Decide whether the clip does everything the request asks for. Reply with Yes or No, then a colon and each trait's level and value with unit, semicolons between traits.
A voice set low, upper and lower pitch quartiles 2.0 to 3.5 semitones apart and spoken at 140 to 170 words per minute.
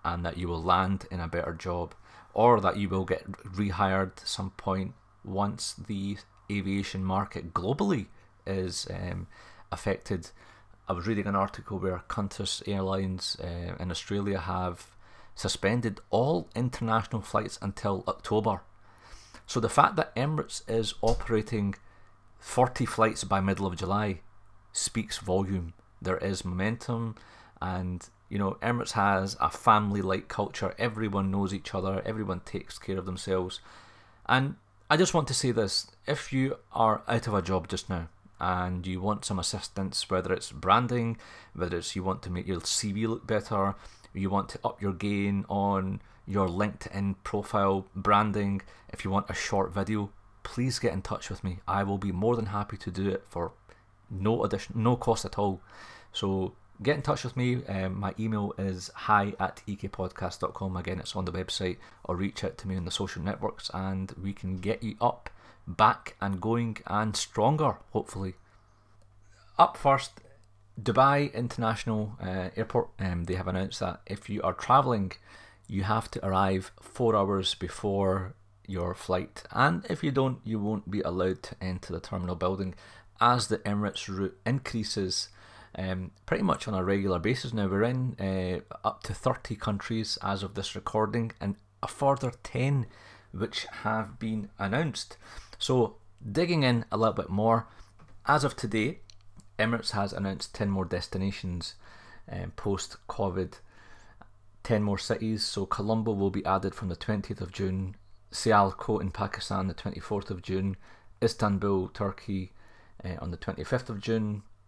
Yes: low, 100 Hz; narrow, 2.6 semitones; average, 160 wpm